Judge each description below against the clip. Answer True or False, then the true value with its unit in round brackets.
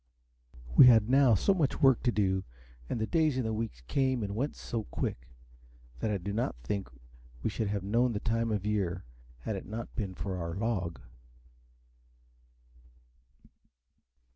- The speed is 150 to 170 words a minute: True (160 wpm)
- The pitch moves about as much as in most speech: True (3.9 semitones)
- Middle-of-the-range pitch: False (110 Hz)